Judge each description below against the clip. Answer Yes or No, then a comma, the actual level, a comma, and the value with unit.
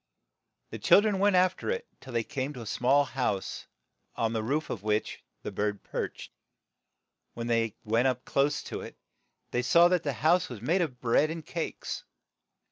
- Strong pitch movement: Yes, wide, 6.3 semitones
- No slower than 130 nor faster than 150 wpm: No, average, 185 wpm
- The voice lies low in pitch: Yes, low, 130 Hz